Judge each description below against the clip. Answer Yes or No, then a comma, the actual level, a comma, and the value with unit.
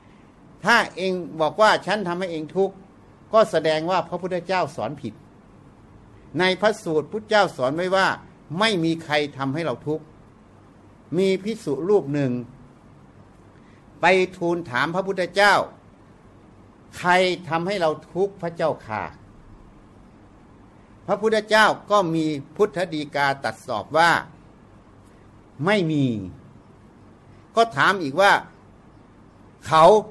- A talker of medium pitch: Yes, medium, 160 Hz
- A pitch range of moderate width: No, wide, 8.8 semitones